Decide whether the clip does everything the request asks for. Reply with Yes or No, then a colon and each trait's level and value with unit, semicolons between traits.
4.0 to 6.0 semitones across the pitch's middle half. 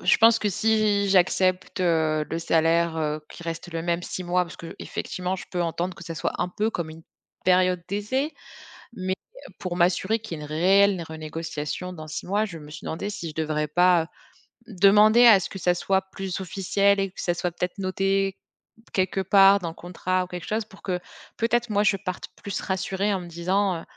No: average, 2.8 semitones